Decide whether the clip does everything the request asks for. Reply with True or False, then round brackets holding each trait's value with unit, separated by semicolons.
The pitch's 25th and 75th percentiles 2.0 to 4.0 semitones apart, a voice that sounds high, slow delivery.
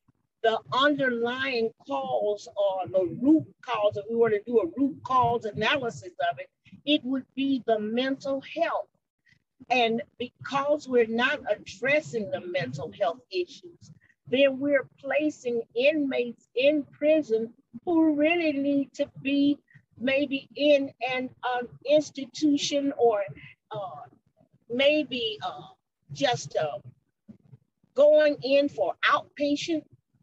False (5.2 semitones; 255 Hz; 115 wpm)